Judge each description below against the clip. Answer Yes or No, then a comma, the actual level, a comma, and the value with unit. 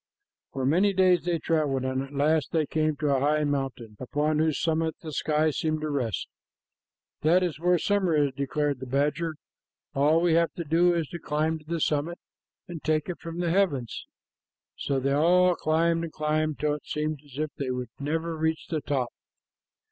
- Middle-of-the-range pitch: Yes, medium, 155 Hz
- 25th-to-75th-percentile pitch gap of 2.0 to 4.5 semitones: Yes, narrow, 2.6 semitones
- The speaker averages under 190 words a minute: No, average, 195 wpm